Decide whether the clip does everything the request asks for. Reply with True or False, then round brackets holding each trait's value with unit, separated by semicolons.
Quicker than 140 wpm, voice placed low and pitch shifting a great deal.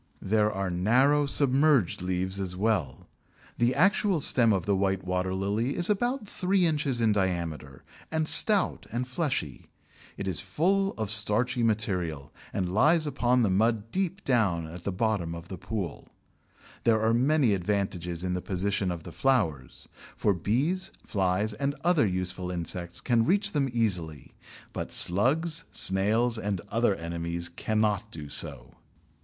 True (150 wpm; 105 Hz; 6.6 semitones)